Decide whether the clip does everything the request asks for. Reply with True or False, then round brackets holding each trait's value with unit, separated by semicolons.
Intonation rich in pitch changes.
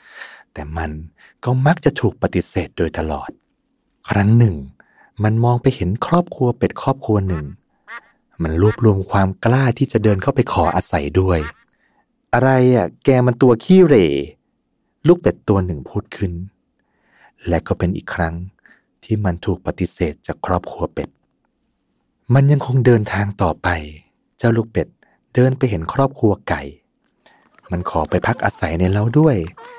True (5.9 semitones)